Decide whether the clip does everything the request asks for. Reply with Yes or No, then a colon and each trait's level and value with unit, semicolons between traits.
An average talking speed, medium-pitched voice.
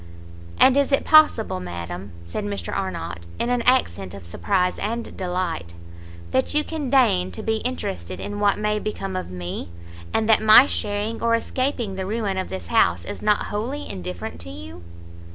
No: average, 175 wpm; high, 195 Hz